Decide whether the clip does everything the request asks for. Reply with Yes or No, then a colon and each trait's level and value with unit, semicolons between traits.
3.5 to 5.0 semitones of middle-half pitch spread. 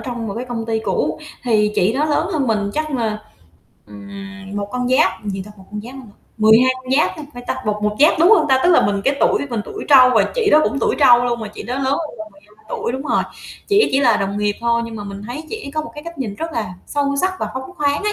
No: wide, 5.4 semitones